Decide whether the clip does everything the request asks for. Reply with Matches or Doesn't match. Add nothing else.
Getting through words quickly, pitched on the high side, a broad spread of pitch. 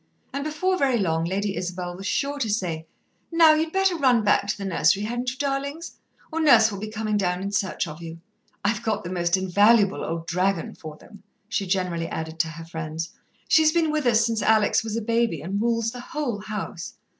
Matches